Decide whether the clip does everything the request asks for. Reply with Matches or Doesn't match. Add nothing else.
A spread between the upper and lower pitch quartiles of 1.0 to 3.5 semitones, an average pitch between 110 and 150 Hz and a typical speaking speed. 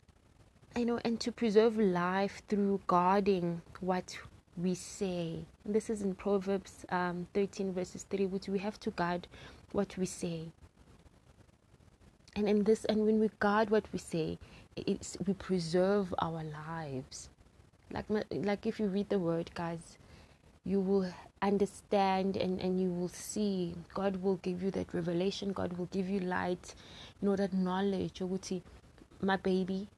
Doesn't match